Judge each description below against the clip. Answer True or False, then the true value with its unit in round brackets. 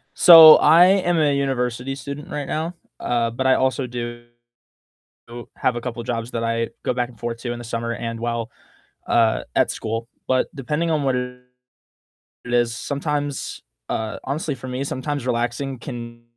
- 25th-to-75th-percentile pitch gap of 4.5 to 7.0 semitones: False (3.0 semitones)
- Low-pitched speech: True (125 Hz)